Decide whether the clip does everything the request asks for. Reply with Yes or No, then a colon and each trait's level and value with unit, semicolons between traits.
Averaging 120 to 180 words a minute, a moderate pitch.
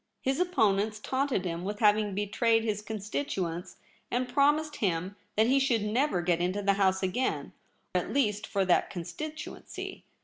No: average, 165 wpm; high, 210 Hz